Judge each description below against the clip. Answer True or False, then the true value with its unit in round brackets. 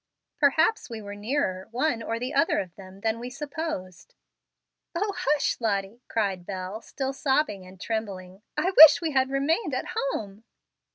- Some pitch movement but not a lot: False (6.4 semitones)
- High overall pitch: True (230 Hz)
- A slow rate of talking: False (160 wpm)